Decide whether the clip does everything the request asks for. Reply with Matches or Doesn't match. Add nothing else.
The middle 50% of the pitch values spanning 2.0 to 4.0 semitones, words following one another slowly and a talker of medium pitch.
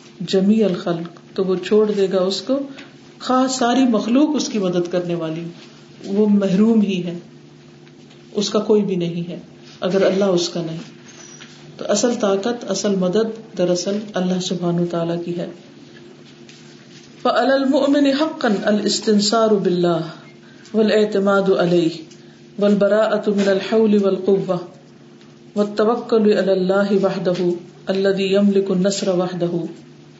Doesn't match